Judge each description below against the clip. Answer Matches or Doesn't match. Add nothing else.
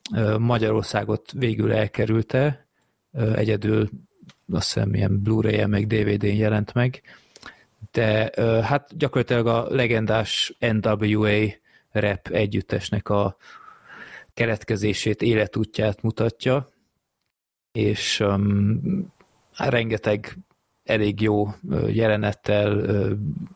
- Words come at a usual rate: Doesn't match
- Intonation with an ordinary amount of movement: Doesn't match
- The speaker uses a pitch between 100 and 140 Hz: Matches